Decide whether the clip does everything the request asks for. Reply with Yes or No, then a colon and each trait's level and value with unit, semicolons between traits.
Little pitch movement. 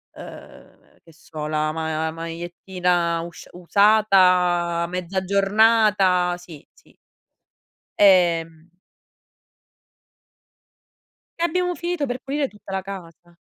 No: average, 3.2 semitones